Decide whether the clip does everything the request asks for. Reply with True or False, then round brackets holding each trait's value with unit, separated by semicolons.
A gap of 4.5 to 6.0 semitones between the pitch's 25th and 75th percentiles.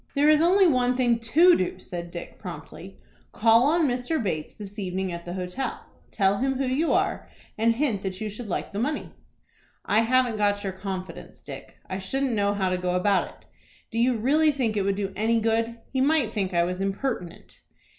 True (5.2 semitones)